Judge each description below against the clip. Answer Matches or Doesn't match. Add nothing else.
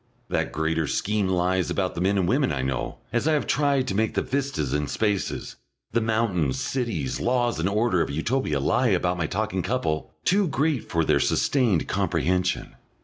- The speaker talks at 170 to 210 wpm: Matches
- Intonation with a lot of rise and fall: Matches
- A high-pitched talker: Doesn't match